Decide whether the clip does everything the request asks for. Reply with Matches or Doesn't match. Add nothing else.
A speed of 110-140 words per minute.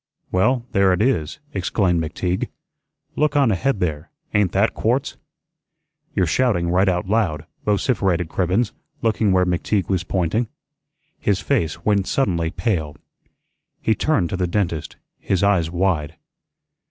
Matches